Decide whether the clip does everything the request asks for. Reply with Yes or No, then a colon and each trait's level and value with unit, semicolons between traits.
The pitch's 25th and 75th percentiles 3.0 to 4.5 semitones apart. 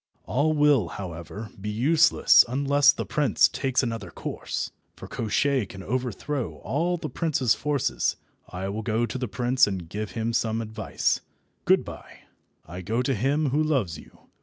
No: average, 5.1 semitones